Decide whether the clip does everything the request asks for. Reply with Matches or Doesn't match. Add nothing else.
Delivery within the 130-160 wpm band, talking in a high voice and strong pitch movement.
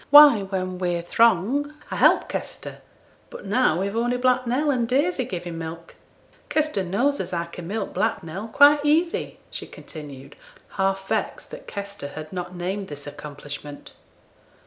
Matches